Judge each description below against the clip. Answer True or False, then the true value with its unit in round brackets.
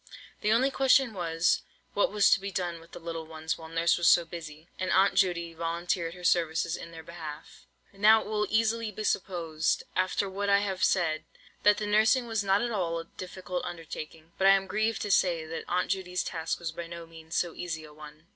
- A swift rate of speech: True (215 wpm)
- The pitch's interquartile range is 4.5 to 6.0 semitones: False (3.4 semitones)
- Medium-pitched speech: True (175 Hz)